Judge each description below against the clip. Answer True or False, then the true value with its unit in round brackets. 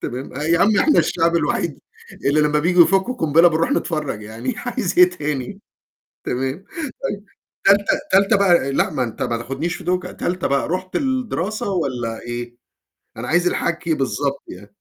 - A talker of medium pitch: True (170 Hz)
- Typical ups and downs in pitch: False (6.0 semitones)